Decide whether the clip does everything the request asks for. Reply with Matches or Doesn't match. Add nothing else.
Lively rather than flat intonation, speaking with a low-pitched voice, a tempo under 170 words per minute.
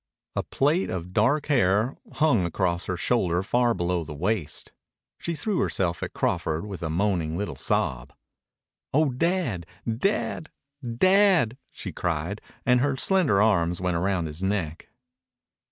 Matches